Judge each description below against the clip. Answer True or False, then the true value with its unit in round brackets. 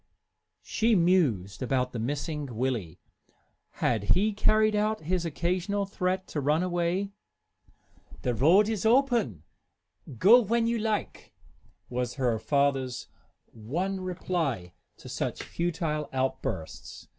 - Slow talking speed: True (115 wpm)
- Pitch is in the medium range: True (170 Hz)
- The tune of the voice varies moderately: False (7.6 semitones)